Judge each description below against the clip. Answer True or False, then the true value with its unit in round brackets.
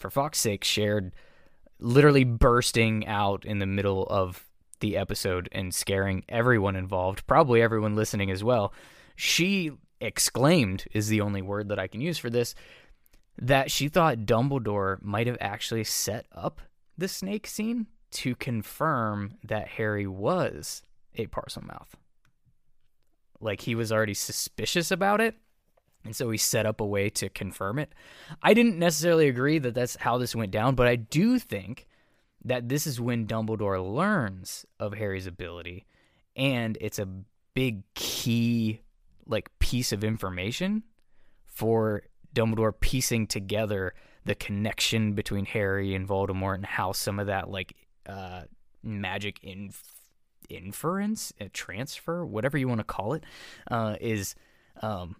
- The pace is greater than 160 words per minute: False (145 wpm)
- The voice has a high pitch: False (110 Hz)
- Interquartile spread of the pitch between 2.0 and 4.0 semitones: False (4.6 semitones)